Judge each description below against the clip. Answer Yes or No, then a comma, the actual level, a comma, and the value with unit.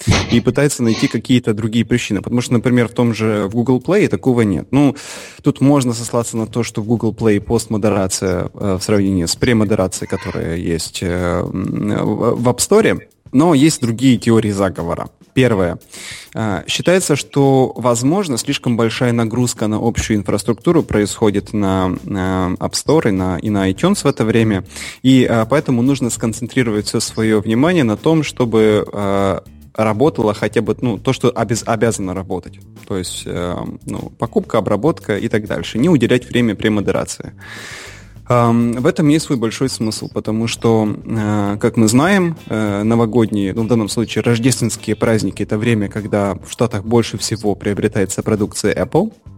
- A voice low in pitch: Yes, low, 115 Hz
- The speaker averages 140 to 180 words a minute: Yes, average, 155 wpm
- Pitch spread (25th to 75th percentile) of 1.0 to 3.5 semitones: Yes, average, 3.2 semitones